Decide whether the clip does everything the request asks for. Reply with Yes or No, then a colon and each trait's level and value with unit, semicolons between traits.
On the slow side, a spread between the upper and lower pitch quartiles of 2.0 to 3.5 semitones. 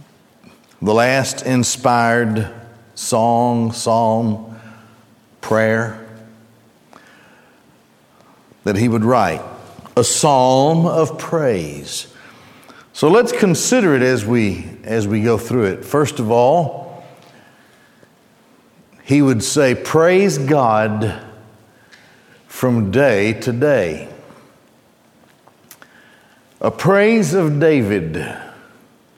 No: slow, 85 wpm; average, 4.2 semitones